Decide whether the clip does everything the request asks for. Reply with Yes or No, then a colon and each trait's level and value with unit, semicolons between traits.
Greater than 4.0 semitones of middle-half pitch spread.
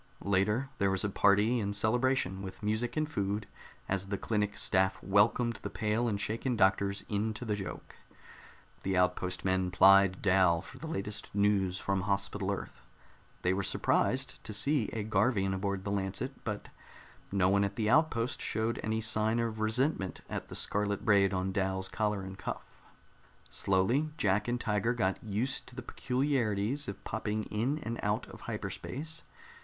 No: average, 3.0 semitones